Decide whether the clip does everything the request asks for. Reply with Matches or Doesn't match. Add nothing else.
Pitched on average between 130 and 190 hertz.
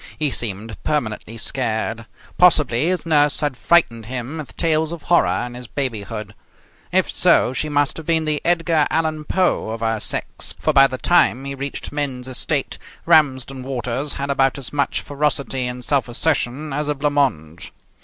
Matches